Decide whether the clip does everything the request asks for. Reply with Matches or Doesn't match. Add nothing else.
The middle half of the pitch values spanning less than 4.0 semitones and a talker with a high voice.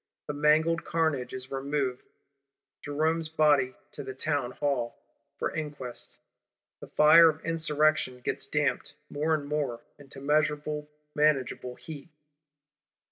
Doesn't match